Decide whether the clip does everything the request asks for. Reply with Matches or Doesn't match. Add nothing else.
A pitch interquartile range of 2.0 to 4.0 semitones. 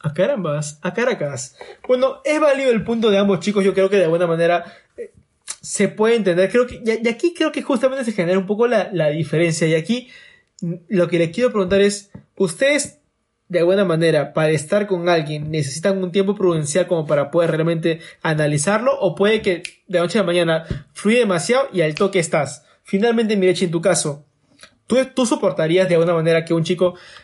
Doesn't match